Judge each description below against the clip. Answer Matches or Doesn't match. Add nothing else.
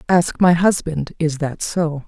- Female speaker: Matches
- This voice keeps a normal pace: Matches